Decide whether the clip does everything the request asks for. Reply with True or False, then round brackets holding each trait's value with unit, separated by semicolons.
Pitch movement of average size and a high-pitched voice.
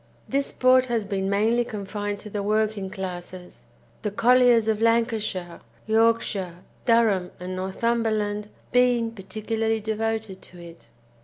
True (3.0 semitones; 215 Hz)